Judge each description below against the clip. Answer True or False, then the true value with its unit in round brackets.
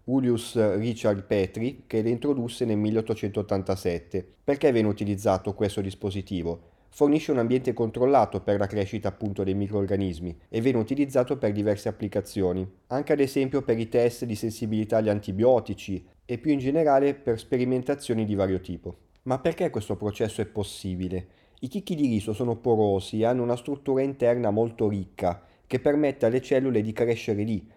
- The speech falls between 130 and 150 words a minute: False (160 wpm)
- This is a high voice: False (110 Hz)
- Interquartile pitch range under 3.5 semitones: False (4.0 semitones)